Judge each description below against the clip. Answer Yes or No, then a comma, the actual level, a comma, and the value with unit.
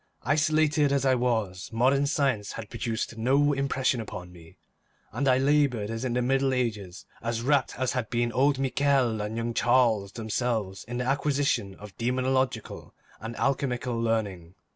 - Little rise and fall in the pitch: No, average, 3.4 semitones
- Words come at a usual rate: Yes, average, 160 wpm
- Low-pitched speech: Yes, low, 125 Hz